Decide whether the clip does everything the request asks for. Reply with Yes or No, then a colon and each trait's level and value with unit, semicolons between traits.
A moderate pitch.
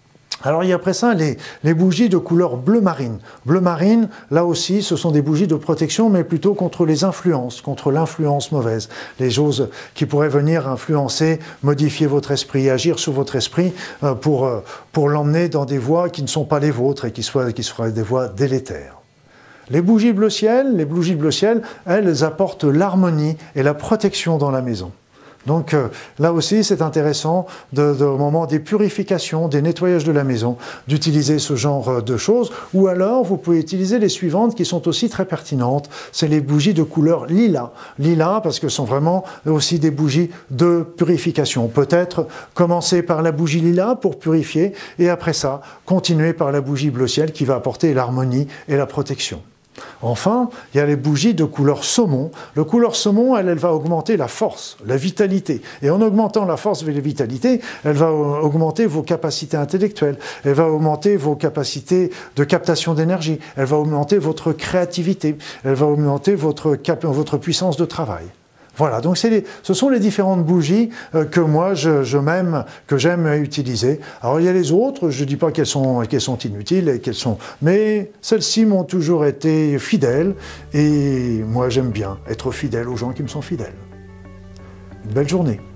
Yes: medium, 155 Hz